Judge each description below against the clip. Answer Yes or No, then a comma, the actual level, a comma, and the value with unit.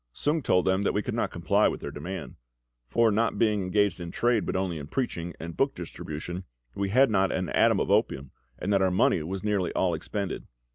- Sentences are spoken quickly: Yes, fast, 220 wpm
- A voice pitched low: Yes, very low, 95 Hz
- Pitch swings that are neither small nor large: Yes, average, 3.2 semitones